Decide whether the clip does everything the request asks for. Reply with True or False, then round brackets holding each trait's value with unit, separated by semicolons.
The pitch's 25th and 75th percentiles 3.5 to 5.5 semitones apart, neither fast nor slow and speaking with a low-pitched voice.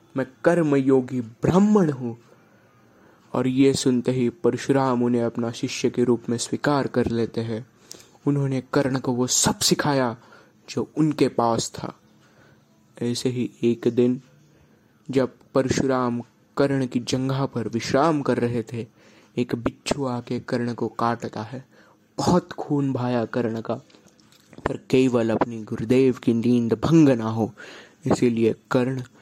False (2.4 semitones; 135 wpm; 125 Hz)